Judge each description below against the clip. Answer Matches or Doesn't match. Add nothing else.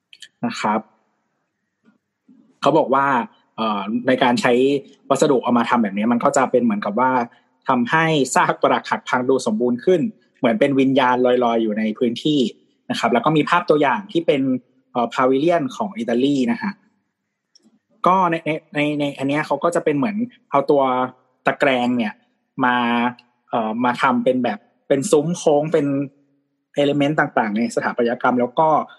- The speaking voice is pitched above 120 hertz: Matches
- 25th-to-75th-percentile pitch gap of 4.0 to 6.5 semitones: Matches